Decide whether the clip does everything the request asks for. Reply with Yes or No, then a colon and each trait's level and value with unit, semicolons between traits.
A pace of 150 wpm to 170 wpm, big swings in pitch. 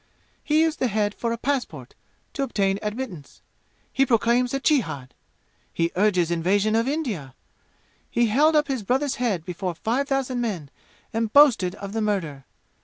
Yes: average, 160 wpm; wide, 5.7 semitones